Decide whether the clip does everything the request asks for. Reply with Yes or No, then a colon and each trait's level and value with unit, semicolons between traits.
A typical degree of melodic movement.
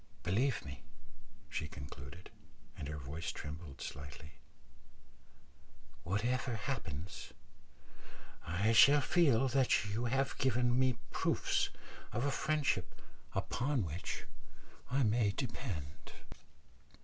No: wide, 8.5 semitones